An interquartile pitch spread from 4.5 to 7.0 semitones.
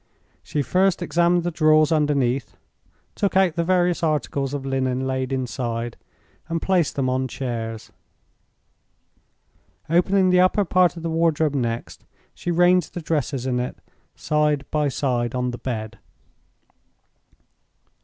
Yes: average, 5.1 semitones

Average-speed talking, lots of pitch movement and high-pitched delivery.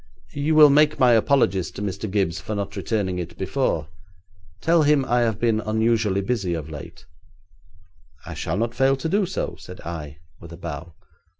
No: average, 180 wpm; wide, 6.7 semitones; low, 110 Hz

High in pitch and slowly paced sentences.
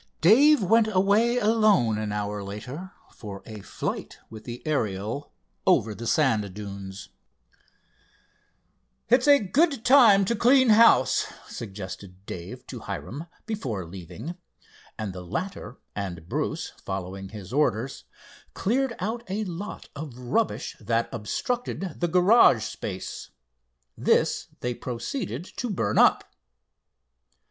No: low, 130 Hz; slow, 120 wpm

